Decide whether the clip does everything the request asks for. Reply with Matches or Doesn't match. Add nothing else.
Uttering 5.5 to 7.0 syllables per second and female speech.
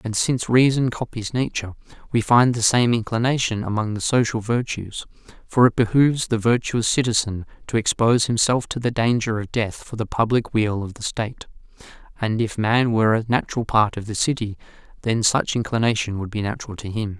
Doesn't match